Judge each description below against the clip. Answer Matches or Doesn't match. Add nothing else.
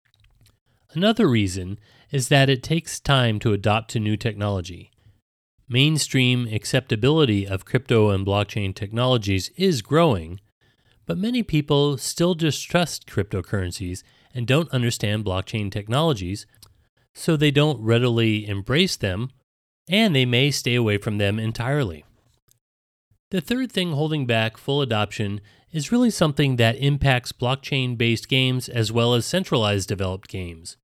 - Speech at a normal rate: Doesn't match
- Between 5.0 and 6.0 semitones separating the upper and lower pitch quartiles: Matches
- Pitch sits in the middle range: Doesn't match